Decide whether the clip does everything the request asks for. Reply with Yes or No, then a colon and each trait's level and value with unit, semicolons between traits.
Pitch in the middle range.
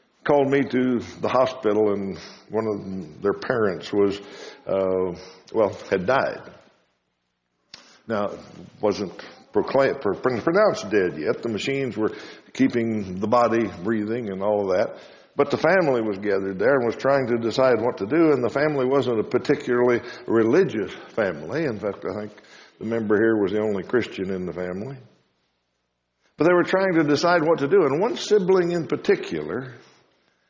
No: low, 115 Hz